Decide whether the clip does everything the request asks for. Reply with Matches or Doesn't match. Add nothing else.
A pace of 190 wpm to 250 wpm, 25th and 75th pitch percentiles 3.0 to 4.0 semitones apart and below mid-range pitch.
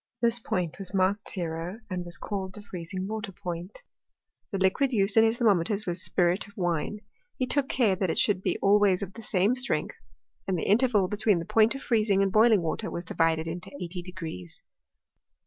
Doesn't match